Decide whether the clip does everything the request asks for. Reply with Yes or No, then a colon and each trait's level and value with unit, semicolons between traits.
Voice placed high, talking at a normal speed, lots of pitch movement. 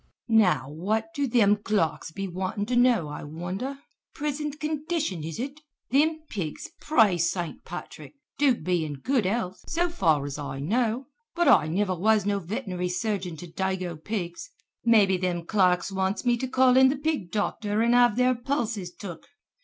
Yes: high, 205 Hz; average, 170 wpm; wide, 6.1 semitones